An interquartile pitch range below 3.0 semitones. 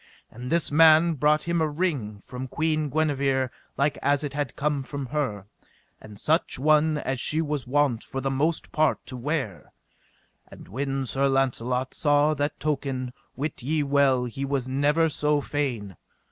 Yes: narrow, 2.6 semitones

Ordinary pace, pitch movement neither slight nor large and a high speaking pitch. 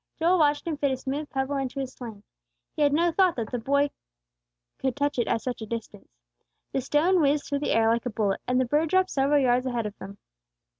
No: fast, 235 wpm; average, 3.5 semitones; very high, 270 Hz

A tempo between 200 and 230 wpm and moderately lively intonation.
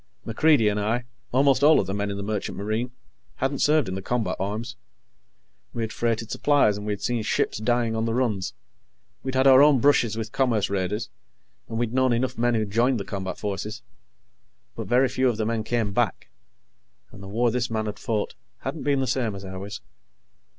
Yes: fast, 205 wpm; average, 3.5 semitones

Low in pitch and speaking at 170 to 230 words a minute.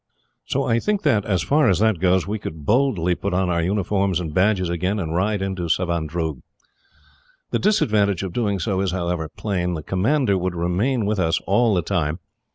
Yes: very low, 95 Hz; average, 190 wpm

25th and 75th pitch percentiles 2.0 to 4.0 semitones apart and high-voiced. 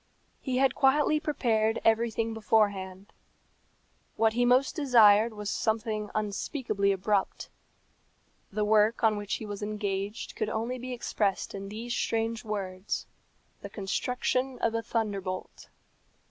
Yes: narrow, 2.5 semitones; high, 220 Hz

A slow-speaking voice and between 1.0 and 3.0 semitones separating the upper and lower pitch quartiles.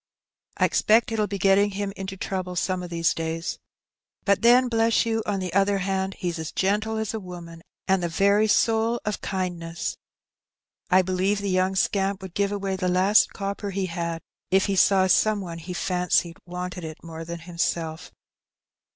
No: average, 180 wpm; narrow, 2.4 semitones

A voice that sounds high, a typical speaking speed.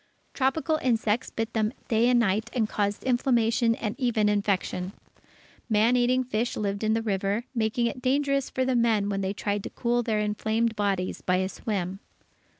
Yes: high, 220 Hz; average, 175 wpm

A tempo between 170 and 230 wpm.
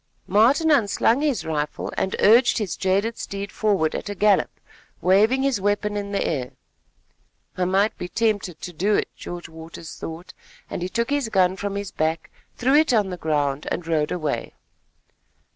Yes: average, 175 wpm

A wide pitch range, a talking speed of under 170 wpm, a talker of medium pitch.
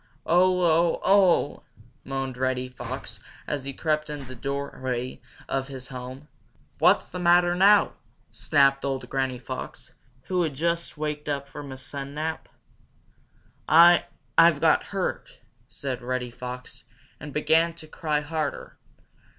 No: average, 3.9 semitones; average, 140 wpm; medium, 145 Hz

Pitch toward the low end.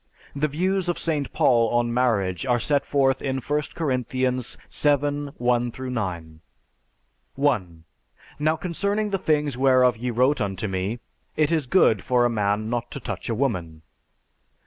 Yes: low, 125 Hz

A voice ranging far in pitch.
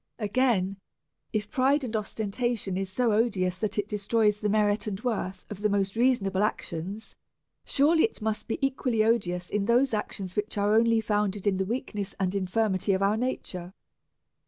No: average, 2.8 semitones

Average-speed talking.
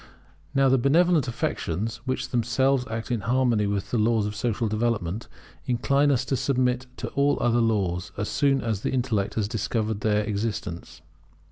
Yes: average, 165 wpm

